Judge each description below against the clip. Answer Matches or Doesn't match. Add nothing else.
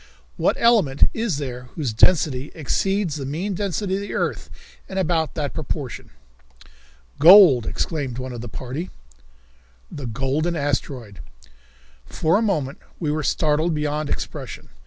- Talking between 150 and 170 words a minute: Doesn't match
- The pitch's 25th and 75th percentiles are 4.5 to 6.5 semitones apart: Matches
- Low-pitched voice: Doesn't match